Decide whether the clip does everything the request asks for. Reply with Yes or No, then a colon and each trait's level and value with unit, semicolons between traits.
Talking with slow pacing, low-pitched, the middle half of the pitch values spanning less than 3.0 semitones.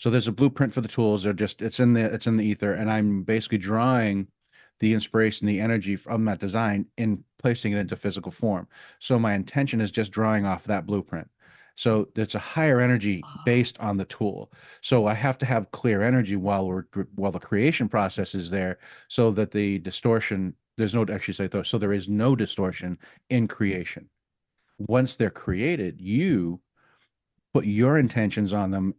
No: average, 190 wpm; low, 105 Hz; narrow, 2.6 semitones